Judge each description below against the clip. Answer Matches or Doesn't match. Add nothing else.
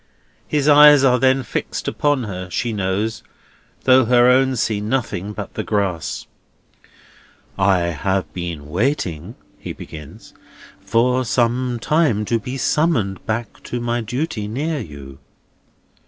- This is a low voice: Matches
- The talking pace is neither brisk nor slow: Doesn't match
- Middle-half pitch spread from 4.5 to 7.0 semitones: Matches